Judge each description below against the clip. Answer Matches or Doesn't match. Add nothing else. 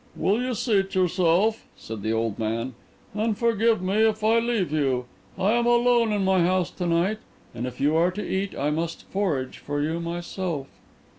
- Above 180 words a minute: Matches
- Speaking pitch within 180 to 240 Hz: Matches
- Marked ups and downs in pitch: Matches